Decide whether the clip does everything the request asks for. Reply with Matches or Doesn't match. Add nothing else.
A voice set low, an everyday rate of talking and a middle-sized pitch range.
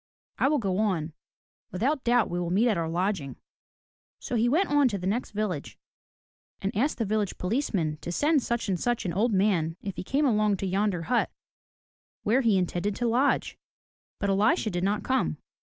Doesn't match